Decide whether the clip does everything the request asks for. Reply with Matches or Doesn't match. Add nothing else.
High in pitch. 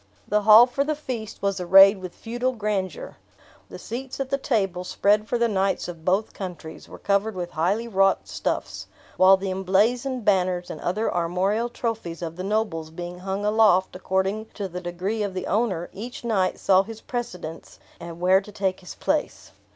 Matches